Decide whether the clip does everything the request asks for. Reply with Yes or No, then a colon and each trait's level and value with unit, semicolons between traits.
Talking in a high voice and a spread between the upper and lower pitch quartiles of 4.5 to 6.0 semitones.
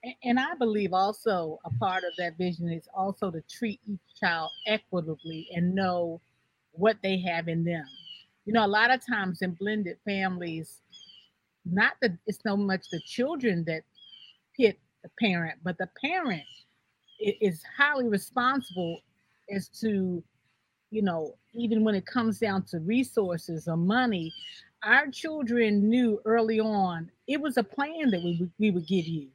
Yes: high, 195 Hz; average, 4.8 semitones